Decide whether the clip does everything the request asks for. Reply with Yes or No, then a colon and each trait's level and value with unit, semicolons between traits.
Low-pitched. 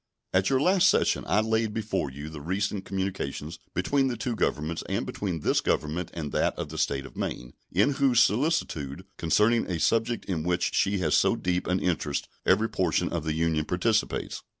Yes: very low, 90 Hz